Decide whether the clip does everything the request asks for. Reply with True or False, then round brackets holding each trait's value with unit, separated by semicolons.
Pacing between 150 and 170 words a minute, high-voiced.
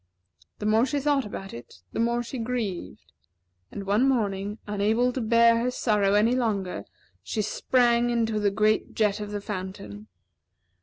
True (155 wpm; 215 Hz)